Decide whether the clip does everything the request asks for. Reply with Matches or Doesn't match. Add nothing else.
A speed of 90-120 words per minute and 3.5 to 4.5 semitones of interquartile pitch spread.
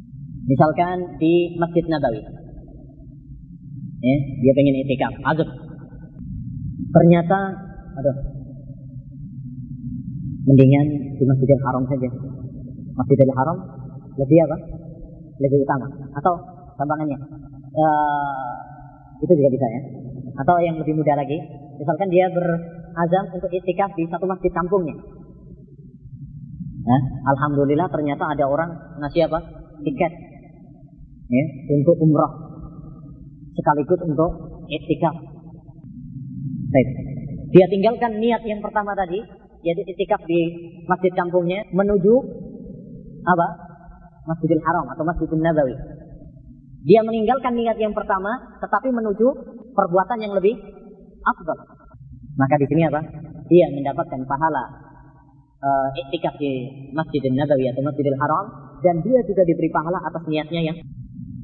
Matches